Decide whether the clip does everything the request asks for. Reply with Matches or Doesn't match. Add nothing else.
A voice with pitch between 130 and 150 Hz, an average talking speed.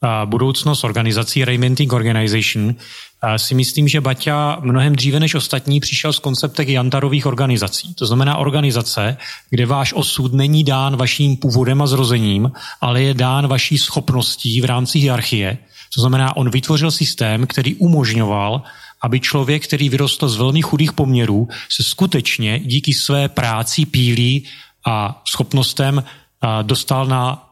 Matches